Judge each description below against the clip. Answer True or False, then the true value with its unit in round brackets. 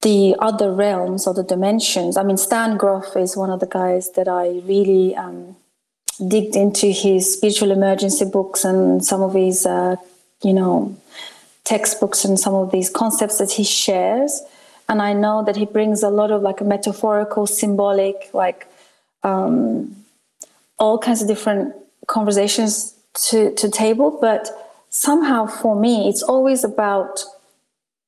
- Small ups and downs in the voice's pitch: True (2.1 semitones)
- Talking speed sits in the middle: True (150 wpm)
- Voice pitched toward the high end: True (205 Hz)